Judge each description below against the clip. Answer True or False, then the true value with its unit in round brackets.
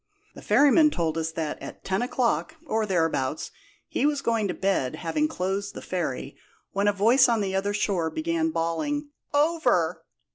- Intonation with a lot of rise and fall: True (8.4 semitones)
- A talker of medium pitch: False (205 Hz)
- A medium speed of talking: True (170 wpm)